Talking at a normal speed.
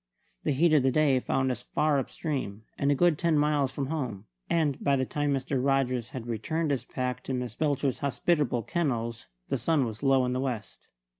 No: fast, 210 wpm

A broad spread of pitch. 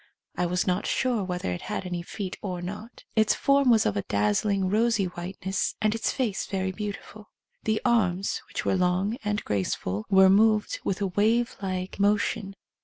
No: average, 3.1 semitones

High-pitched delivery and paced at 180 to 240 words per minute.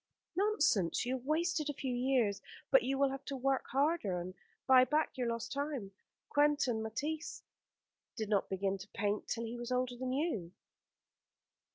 No: very high, 255 Hz; average, 170 wpm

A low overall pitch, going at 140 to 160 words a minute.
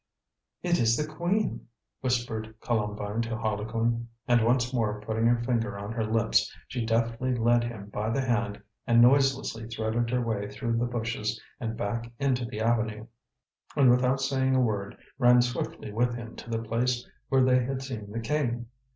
No: low, 115 Hz; average, 175 wpm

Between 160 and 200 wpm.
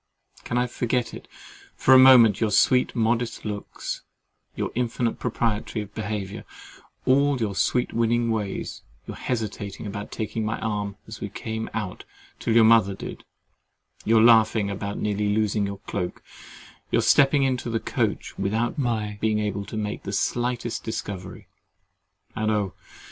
No: average, 140 wpm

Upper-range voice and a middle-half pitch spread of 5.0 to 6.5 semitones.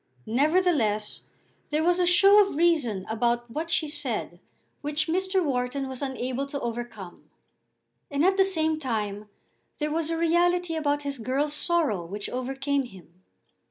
Yes: very high, 285 Hz; wide, 5.6 semitones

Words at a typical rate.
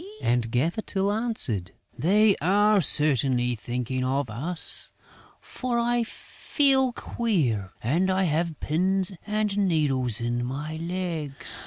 No: slow, 120 wpm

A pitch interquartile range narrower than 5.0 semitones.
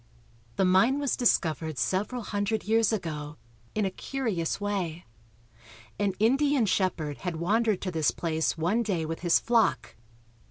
No: wide, 5.4 semitones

